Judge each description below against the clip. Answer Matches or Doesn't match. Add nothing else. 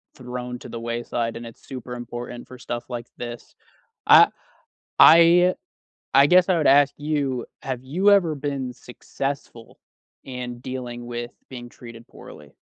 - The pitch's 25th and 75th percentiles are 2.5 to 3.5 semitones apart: Matches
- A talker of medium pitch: Doesn't match